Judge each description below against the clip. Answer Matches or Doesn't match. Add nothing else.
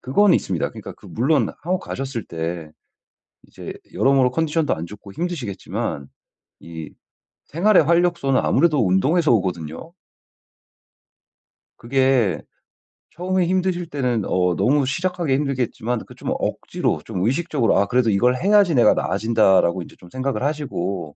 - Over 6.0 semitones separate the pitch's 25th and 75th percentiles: Matches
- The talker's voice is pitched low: Matches